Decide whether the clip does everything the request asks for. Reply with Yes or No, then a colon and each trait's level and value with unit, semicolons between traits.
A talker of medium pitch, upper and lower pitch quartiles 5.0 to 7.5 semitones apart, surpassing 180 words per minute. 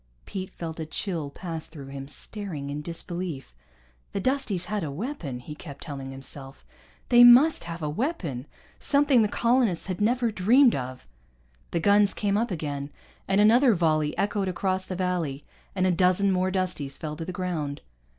No: medium, 180 Hz; wide, 5.6 semitones; average, 170 wpm